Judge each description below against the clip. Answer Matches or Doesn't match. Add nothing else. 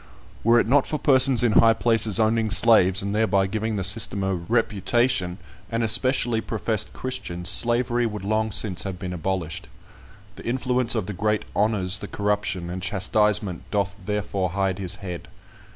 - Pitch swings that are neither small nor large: Matches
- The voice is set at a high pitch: Doesn't match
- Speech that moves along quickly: Doesn't match